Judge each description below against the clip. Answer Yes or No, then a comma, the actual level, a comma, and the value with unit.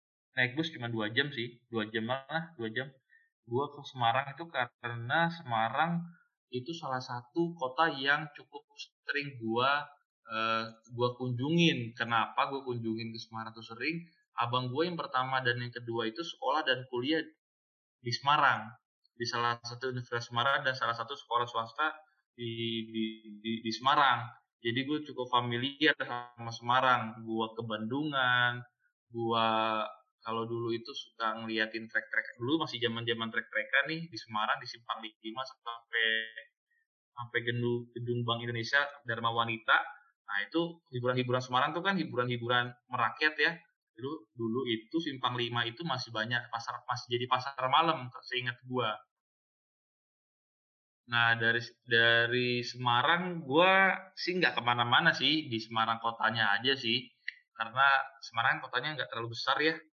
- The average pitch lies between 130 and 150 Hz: No, low, 120 Hz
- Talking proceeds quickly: Yes, fast, 145 wpm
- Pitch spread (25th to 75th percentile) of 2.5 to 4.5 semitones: Yes, average, 3.8 semitones